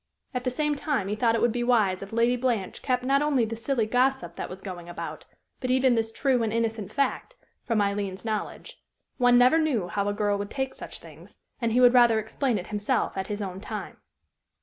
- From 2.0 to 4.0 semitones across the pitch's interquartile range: Yes, average, 3.6 semitones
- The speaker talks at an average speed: No, fast, 220 wpm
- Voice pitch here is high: Yes, high, 230 Hz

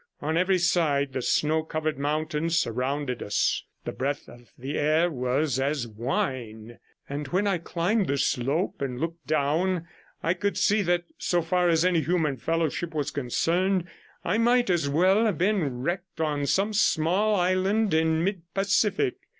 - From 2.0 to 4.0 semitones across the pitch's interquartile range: No, average, 4.6 semitones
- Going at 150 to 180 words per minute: Yes, average, 160 wpm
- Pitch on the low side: No, medium, 160 Hz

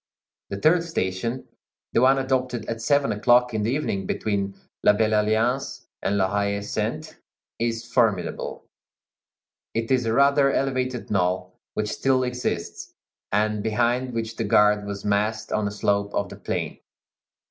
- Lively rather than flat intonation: No, average, 3.7 semitones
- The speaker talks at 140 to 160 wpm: Yes, average, 150 wpm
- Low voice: Yes, low, 110 Hz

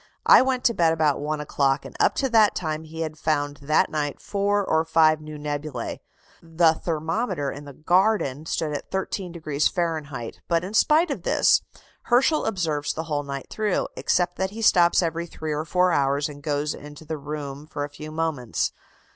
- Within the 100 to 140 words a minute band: No, average, 190 wpm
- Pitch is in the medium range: Yes, medium, 155 Hz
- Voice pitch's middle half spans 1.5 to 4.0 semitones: Yes, average, 3.4 semitones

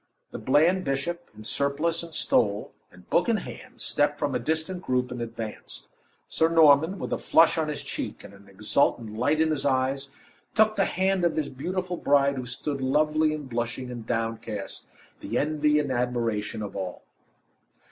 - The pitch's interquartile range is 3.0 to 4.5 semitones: No, average, 5.2 semitones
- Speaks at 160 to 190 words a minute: Yes, average, 175 wpm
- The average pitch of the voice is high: No, medium, 140 Hz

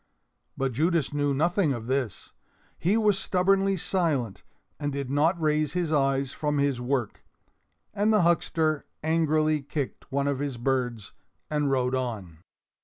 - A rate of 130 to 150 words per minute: Yes, average, 145 wpm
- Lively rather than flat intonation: No, average, 3.8 semitones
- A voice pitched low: No, medium, 145 Hz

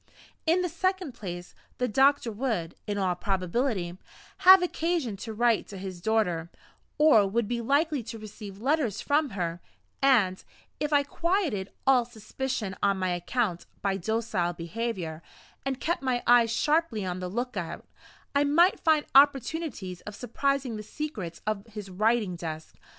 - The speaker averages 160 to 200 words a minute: No, average, 150 wpm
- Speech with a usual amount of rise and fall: No, wide, 6.6 semitones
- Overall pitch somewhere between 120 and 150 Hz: No, high, 225 Hz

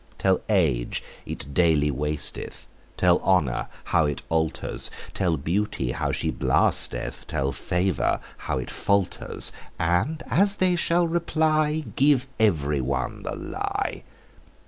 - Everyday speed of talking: No, slow, 125 wpm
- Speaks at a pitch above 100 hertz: No, very low, 90 Hz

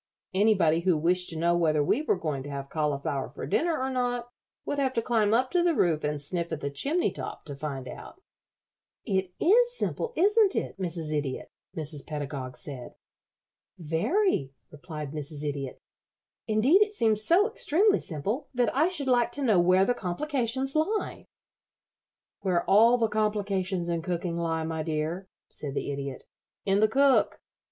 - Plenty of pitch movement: Yes, wide, 8.9 semitones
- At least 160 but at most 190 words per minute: Yes, average, 170 wpm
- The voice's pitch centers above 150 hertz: Yes, medium, 185 Hz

